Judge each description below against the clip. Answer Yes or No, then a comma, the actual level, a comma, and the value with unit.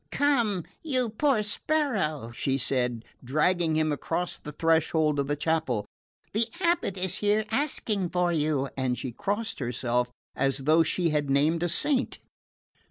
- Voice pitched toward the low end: No, medium, 165 Hz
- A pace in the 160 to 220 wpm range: No, average, 150 wpm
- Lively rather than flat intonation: Yes, wide, 7.0 semitones